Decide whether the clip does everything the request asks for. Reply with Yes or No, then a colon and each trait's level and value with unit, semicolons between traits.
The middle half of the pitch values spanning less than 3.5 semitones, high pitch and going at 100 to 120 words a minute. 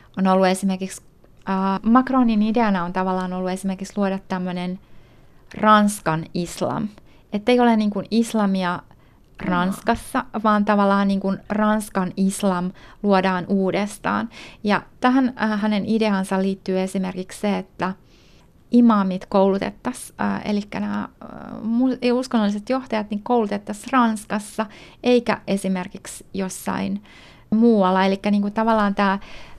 Yes: narrow, 2.4 semitones; high, 200 Hz; average, 115 wpm